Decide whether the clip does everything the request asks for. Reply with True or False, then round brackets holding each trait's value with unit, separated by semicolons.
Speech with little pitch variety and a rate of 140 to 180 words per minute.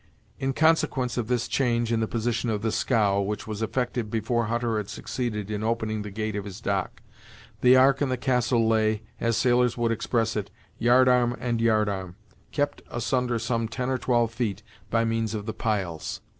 False (2.3 semitones; 195 wpm)